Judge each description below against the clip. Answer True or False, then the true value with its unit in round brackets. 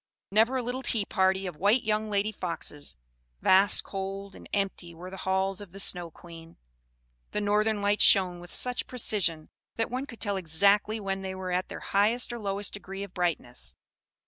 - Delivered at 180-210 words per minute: True (185 wpm)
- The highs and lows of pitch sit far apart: False (2.6 semitones)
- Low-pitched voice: False (195 Hz)